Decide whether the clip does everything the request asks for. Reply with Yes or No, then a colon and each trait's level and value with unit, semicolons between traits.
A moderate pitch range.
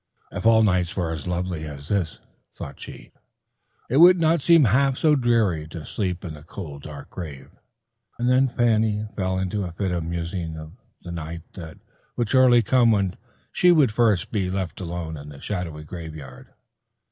No: wide, 6.1 semitones